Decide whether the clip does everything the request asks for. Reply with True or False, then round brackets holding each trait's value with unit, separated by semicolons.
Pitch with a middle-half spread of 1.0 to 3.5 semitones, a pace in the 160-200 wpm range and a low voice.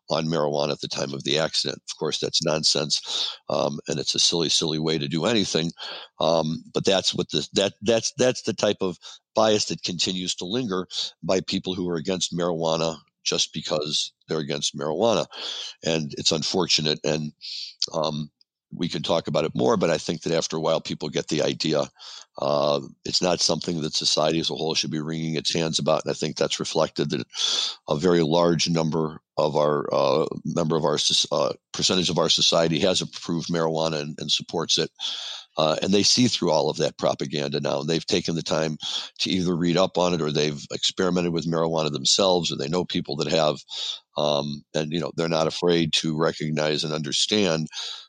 True (2.4 semitones; 195 wpm; 80 Hz)